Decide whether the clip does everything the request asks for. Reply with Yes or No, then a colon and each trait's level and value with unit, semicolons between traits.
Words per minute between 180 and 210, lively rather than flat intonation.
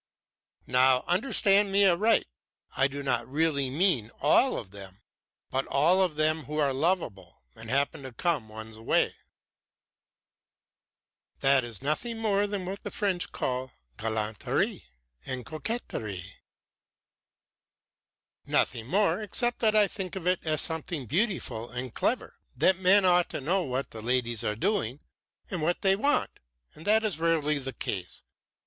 No: average, 150 wpm; wide, 7.2 semitones